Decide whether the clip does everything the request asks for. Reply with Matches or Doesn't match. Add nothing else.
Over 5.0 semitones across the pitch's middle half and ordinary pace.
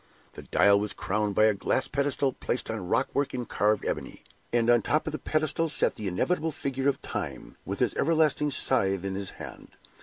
Doesn't match